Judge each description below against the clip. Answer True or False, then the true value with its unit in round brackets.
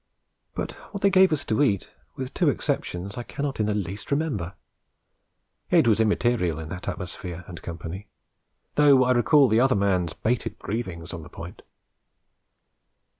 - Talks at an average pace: True (160 wpm)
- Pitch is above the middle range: False (105 Hz)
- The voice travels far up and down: True (6.4 semitones)